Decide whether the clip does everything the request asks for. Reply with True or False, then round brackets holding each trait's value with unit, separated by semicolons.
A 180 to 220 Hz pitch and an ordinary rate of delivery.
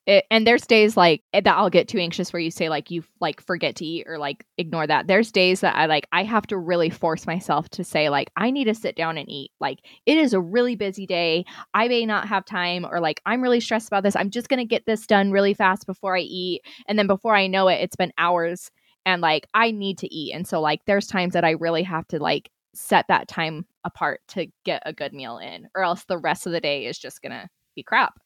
False (185 Hz; 265 wpm)